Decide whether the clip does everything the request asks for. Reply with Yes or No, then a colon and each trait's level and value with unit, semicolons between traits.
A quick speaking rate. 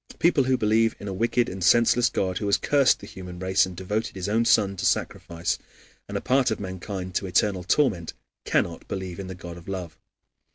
Yes: fast, 210 wpm